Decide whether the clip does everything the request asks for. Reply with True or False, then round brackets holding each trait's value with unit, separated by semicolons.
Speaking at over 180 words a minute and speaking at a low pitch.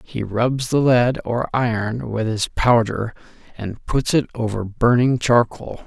False (155 wpm; 115 Hz)